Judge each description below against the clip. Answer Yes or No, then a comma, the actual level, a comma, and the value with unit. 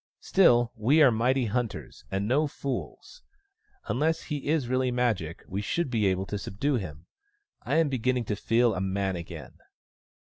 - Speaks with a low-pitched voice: Yes, low, 120 Hz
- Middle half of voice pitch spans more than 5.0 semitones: Yes, wide, 5.5 semitones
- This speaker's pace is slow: No, average, 170 wpm